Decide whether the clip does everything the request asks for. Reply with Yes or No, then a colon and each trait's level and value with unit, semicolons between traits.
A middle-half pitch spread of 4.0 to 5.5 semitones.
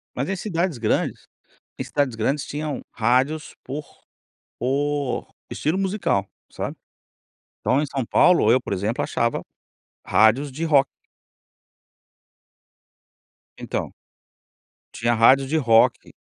Yes: average, 4.5 semitones